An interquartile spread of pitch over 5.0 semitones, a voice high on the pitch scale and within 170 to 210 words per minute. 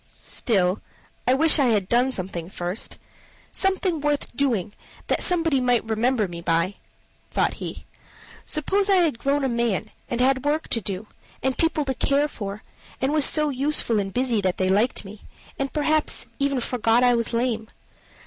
Yes: wide, 5.4 semitones; very high, 250 Hz; average, 175 wpm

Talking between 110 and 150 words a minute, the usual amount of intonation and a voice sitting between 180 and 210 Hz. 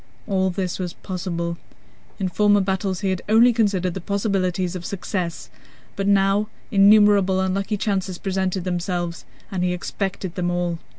No: average, 145 wpm; narrow, 1.9 semitones; high, 190 Hz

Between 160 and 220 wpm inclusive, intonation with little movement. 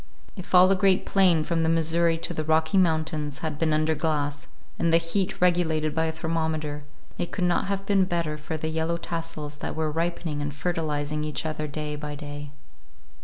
Yes: average, 195 wpm; narrow, 1.9 semitones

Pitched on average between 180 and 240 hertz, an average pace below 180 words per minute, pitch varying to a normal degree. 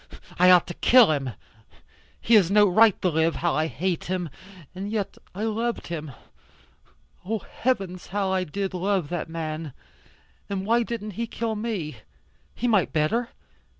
Yes: high, 190 Hz; average, 160 wpm; average, 4.6 semitones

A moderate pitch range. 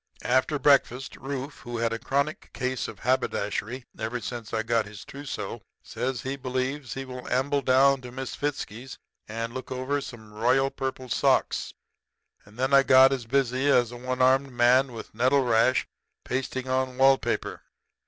No: narrow, 1.8 semitones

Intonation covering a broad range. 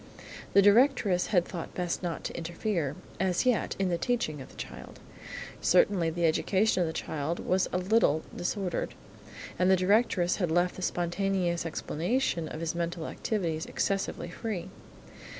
No: average, 2.8 semitones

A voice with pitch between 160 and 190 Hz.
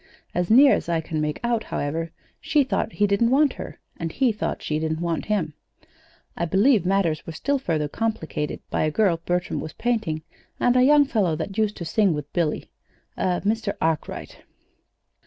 Yes: medium, 185 Hz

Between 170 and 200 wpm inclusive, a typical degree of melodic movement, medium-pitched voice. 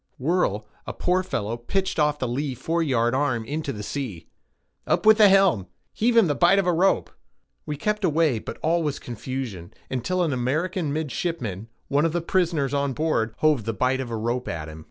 No: average, 195 wpm; wide, 6.4 semitones; medium, 145 Hz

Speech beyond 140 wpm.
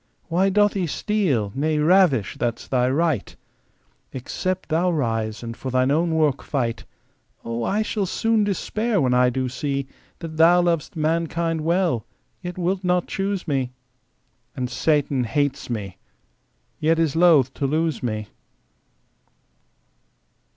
No: slow, 135 wpm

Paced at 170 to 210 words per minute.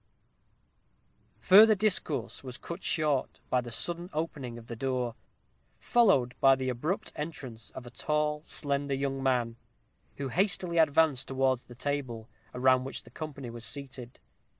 No: average, 145 wpm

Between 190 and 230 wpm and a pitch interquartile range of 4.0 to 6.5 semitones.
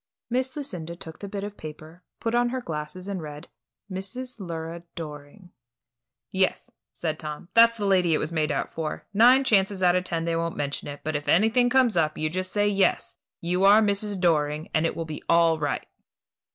Yes: average, 200 wpm; average, 4.6 semitones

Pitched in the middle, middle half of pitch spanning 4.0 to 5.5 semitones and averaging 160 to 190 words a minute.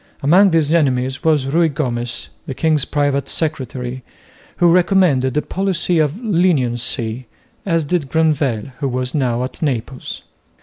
No: medium, 145 Hz; average, 4.5 semitones; slow, 135 wpm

